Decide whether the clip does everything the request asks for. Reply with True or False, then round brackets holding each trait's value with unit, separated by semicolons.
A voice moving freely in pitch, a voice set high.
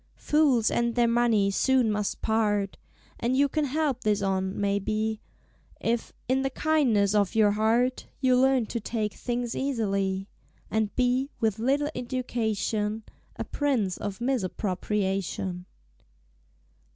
False (3.9 semitones; 225 Hz)